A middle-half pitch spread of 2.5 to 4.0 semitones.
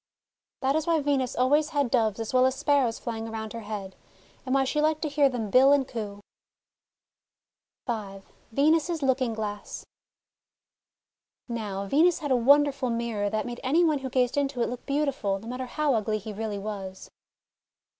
No: average, 4.6 semitones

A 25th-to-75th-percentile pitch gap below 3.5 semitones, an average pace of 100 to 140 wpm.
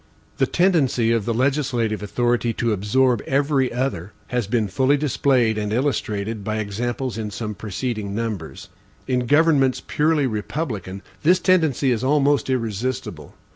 No: average, 4.2 semitones; slow, 135 wpm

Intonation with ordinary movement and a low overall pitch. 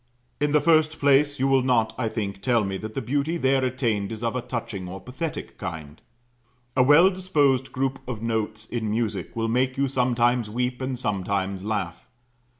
Yes: average, 3.8 semitones; low, 125 Hz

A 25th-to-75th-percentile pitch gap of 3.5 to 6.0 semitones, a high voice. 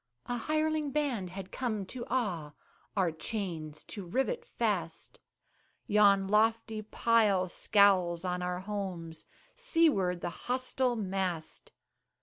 Yes: average, 5.3 semitones; high, 200 Hz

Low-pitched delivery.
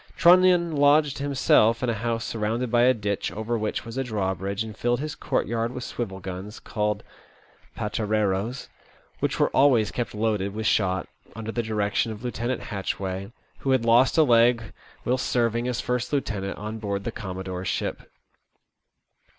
Yes: low, 115 Hz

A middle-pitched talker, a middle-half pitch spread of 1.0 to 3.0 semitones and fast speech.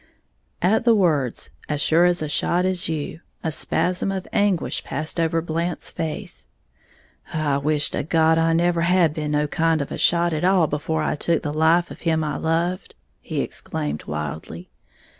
No: medium, 160 Hz; narrow, 2.6 semitones; average, 175 wpm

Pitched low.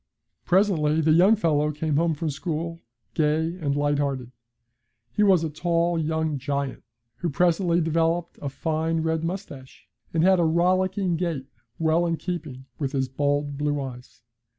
No: medium, 160 Hz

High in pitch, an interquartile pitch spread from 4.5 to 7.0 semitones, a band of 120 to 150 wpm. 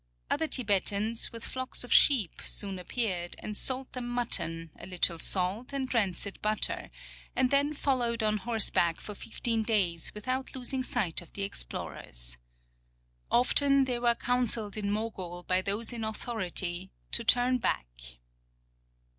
Yes: high, 220 Hz; average, 4.8 semitones; average, 140 wpm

